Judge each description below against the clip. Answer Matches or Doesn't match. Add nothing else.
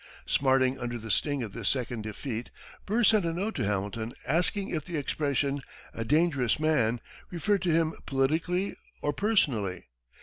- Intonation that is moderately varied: Doesn't match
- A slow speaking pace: Doesn't match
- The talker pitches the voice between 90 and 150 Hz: Matches